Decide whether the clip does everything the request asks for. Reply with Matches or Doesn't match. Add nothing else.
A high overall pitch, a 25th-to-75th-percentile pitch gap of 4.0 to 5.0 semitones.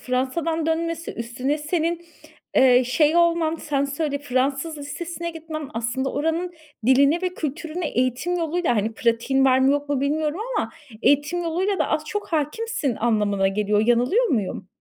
Matches